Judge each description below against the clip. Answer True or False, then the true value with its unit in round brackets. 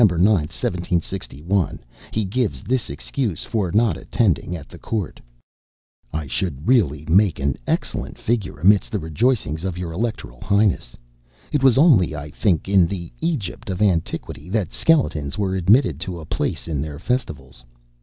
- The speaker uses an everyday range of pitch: False (5.8 semitones)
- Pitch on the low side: True (95 Hz)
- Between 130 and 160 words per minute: True (155 wpm)